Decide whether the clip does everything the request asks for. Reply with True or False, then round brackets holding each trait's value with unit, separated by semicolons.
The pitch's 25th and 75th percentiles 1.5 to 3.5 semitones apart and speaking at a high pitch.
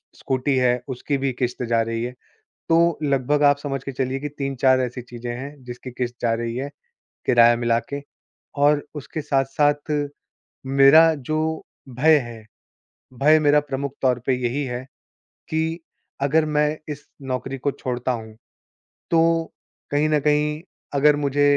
False (2.9 semitones; 135 Hz)